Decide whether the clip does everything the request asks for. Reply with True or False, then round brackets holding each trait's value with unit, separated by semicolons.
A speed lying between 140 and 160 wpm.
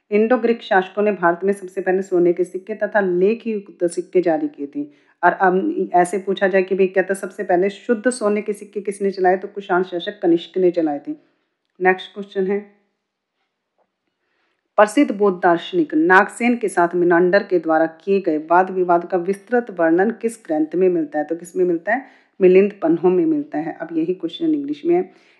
False (190 wpm)